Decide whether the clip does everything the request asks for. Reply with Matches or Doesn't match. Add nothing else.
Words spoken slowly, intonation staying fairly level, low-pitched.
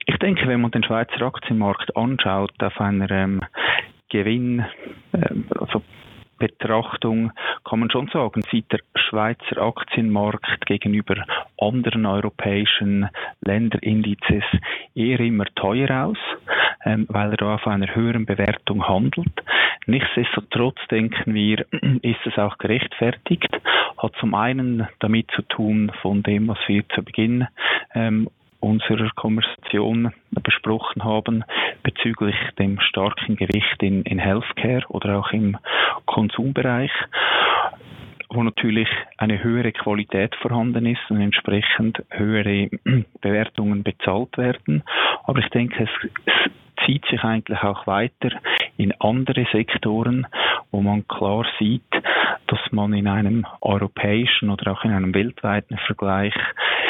Matches